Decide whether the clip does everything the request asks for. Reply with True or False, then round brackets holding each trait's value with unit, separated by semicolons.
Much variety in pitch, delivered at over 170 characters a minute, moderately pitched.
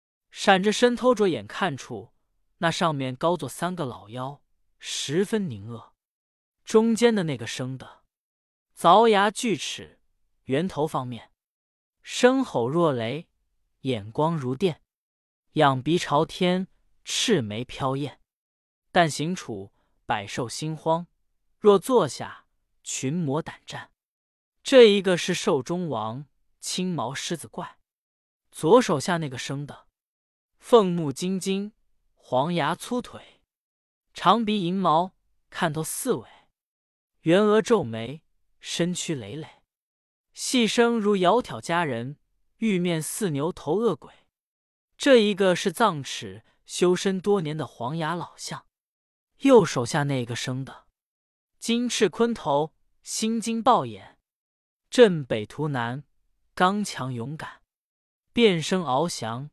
False (7.2 semitones; 165 characters per minute; 165 Hz)